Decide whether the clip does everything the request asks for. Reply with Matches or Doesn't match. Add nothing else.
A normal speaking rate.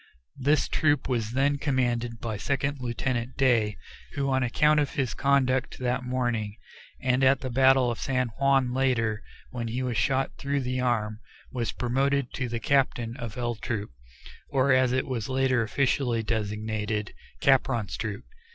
Matches